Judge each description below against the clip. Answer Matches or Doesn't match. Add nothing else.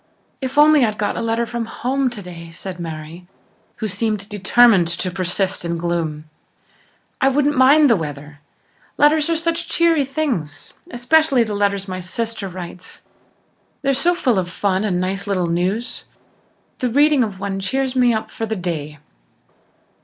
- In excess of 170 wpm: Doesn't match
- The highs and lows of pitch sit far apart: Matches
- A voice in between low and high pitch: Doesn't match